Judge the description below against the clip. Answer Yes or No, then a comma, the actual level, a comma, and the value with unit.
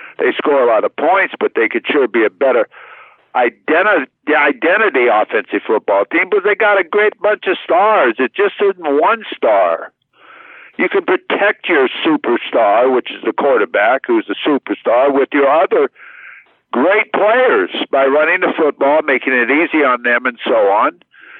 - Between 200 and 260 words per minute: No, average, 170 wpm